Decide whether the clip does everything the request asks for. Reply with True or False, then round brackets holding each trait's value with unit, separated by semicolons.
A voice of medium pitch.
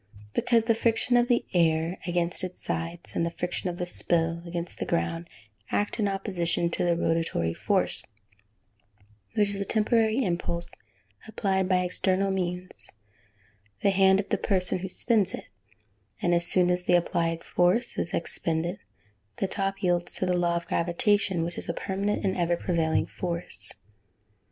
True (180 Hz)